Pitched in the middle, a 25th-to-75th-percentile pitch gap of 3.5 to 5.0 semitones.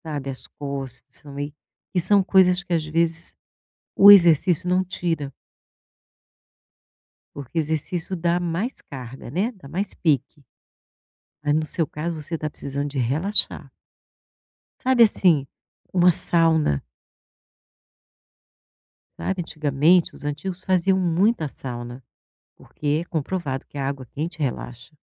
Yes: medium, 160 Hz; average, 4.1 semitones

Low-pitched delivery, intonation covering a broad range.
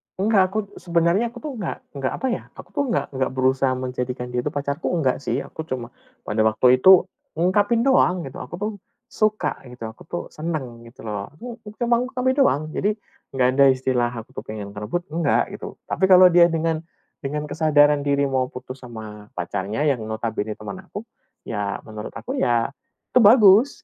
No: medium, 145 Hz; wide, 7.4 semitones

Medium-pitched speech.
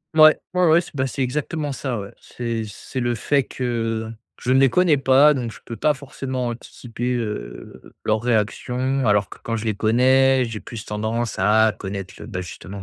No: low, 120 Hz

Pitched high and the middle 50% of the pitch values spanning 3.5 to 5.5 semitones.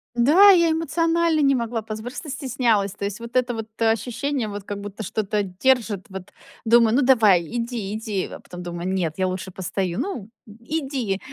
Yes: high, 225 Hz; average, 5.0 semitones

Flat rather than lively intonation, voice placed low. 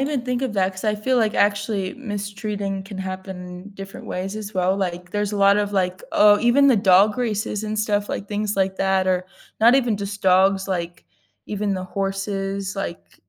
No: narrow, 1.8 semitones; high, 200 Hz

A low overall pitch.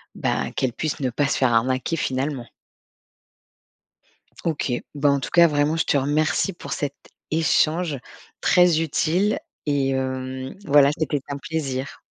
No: medium, 145 Hz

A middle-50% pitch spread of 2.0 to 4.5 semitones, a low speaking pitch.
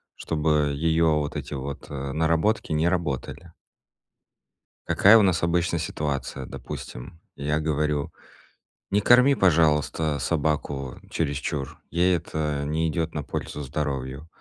Yes: narrow, 2.5 semitones; very low, 75 Hz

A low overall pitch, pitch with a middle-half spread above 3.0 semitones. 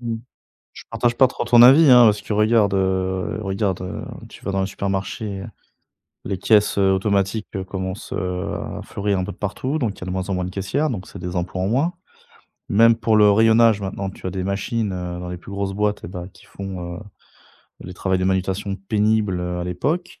No: low, 100 Hz; average, 2.7 semitones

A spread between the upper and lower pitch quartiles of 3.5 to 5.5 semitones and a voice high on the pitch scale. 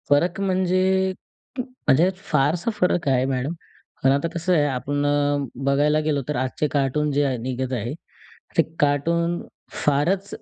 No: average, 4.0 semitones; medium, 145 Hz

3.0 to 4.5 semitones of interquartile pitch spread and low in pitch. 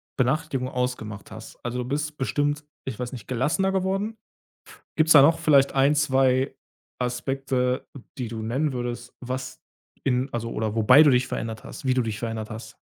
Yes: average, 3.3 semitones; low, 130 Hz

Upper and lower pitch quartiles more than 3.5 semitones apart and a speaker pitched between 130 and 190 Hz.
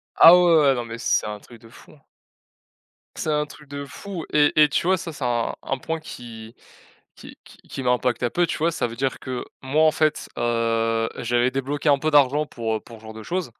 Yes: average, 4.6 semitones; low, 135 Hz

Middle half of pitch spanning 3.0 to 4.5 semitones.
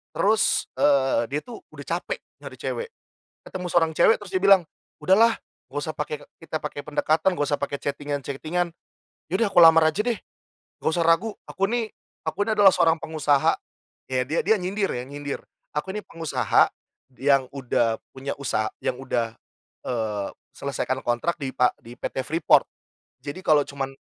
No: average, 5.3 semitones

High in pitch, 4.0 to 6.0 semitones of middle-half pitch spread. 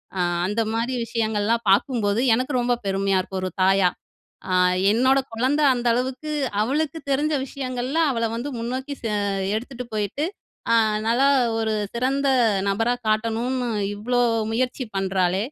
No: high, 235 Hz; average, 3.5 semitones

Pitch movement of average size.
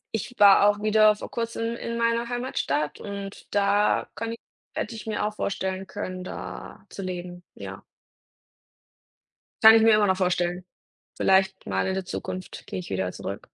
Yes: average, 3.2 semitones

